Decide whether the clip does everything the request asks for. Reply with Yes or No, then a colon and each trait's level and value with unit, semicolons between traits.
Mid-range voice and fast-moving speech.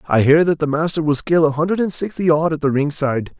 Yes: medium, 155 Hz; fast, 280 wpm